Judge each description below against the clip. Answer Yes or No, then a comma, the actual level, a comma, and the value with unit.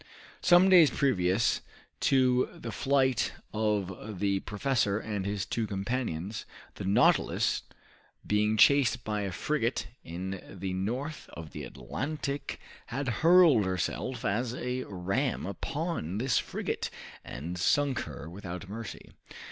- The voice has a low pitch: Yes, low, 110 Hz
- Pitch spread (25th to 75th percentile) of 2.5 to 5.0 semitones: No, wide, 5.4 semitones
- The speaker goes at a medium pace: No, slow, 125 wpm